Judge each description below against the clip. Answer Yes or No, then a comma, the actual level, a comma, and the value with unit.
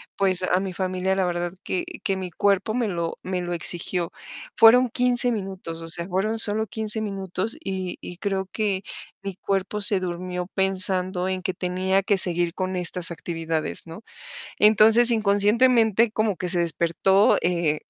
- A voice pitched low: No, high, 190 Hz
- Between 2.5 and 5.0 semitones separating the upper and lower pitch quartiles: Yes, average, 2.9 semitones